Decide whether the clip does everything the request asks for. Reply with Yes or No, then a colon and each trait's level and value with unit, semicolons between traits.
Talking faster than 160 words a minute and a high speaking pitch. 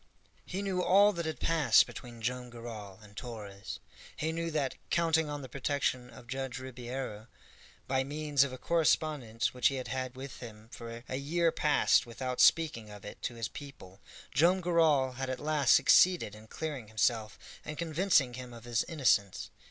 No: average, 175 wpm; low, 130 Hz